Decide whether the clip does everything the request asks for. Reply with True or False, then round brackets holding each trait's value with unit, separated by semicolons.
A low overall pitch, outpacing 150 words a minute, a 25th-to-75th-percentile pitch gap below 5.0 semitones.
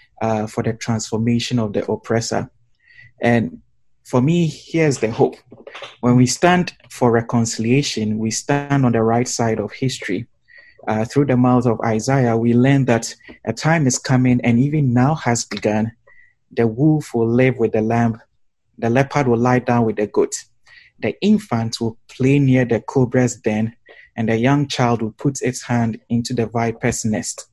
True (120 Hz; 170 wpm; 2.8 semitones)